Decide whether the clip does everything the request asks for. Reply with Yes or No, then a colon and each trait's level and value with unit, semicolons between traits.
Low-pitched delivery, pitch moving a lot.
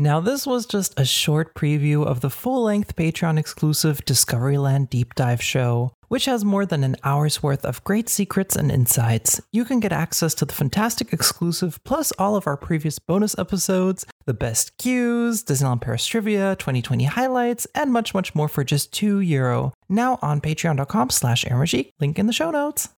No: medium, 155 Hz; wide, 7.1 semitones